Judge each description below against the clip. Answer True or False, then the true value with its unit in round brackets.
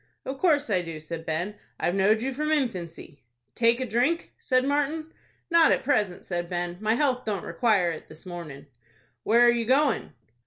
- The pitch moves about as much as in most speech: False (7.5 semitones)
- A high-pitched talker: True (220 Hz)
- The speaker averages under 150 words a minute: False (185 wpm)